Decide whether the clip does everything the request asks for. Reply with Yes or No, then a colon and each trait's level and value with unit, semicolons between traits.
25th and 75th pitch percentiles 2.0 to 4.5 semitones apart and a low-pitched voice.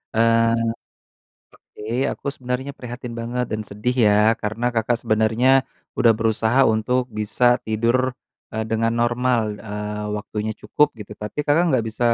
Yes: narrow, 2.4 semitones; low, 115 Hz